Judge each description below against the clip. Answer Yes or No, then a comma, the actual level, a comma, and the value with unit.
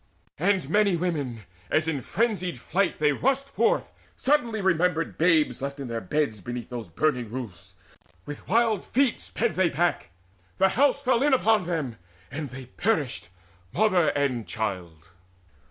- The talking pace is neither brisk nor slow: Yes, average, 150 wpm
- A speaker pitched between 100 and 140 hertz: No, medium, 160 Hz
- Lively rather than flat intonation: Yes, wide, 8.8 semitones